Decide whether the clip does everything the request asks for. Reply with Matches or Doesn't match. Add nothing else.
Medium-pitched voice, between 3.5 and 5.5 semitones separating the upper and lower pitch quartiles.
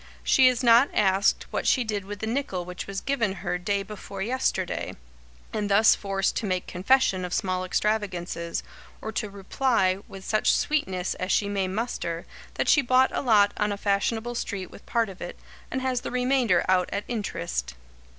Doesn't match